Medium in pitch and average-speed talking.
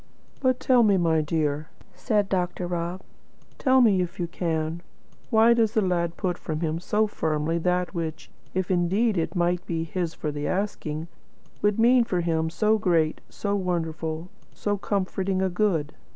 Yes: medium, 180 Hz; average, 165 wpm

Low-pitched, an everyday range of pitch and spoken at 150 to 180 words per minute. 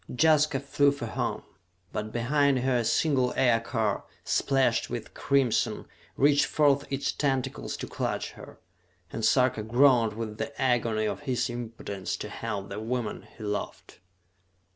No: low, 125 Hz; average, 3.8 semitones; average, 140 wpm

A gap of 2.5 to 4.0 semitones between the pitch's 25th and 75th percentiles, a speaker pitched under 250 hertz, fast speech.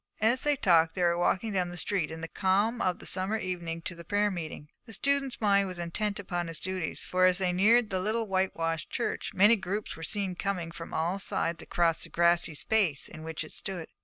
Yes: average, 3.3 semitones; medium, 185 Hz; fast, 225 wpm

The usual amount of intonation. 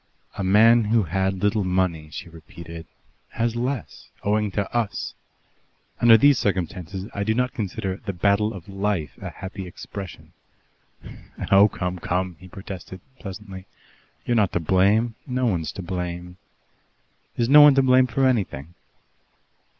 Yes: average, 3.8 semitones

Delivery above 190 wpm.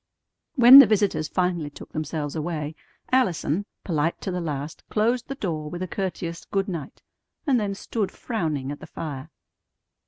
No: average, 160 wpm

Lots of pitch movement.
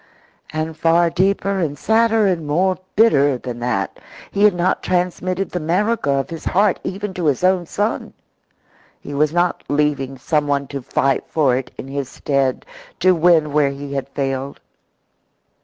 No: average, 4.8 semitones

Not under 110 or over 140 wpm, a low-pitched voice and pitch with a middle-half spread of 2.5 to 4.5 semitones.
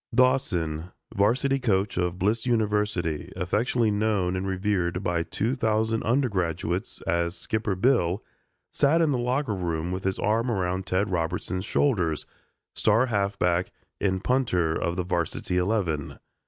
Yes: slow, 135 wpm; very low, 95 Hz; average, 4.1 semitones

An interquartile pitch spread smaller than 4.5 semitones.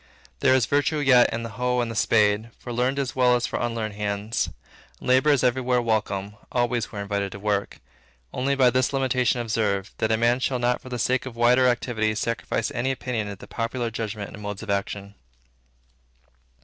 Yes: average, 3.0 semitones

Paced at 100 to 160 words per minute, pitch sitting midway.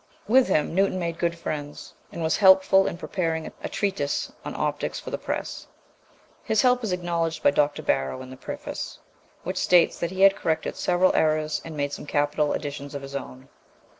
No: average, 190 wpm; medium, 165 Hz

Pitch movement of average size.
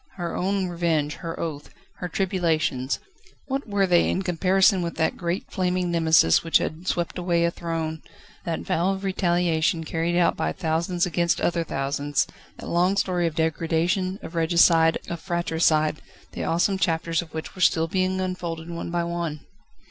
No: narrow, 2.0 semitones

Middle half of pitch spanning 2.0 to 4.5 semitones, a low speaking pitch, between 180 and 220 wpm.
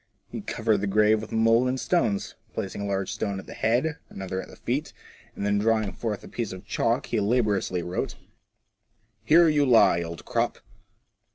Yes: average, 2.9 semitones; low, 105 Hz; average, 190 wpm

